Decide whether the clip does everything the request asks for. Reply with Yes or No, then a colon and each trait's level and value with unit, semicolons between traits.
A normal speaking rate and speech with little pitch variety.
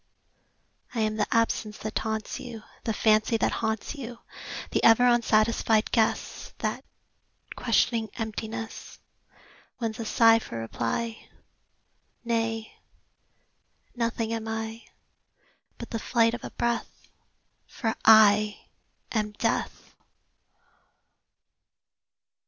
No: slow, 100 wpm; narrow, 1.1 semitones